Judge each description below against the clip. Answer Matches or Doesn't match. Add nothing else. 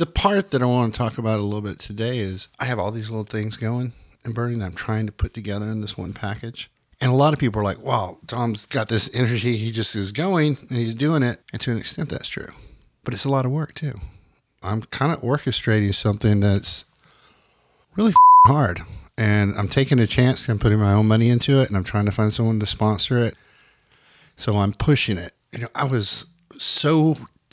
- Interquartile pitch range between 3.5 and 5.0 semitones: Matches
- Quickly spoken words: Matches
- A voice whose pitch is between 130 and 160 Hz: Doesn't match